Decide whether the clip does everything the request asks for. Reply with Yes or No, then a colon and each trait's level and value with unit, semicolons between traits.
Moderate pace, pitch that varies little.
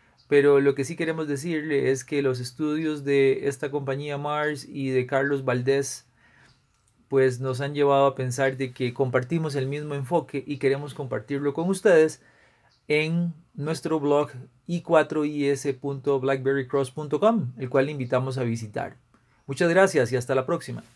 Yes: average, 145 wpm; narrow, 2.2 semitones